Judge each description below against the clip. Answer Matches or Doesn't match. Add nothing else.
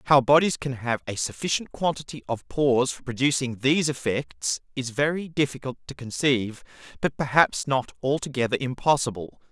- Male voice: Matches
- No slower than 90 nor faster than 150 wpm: Matches